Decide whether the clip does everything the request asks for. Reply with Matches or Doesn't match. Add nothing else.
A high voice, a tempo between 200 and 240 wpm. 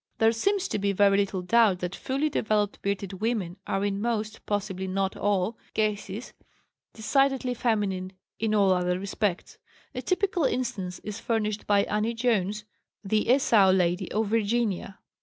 Doesn't match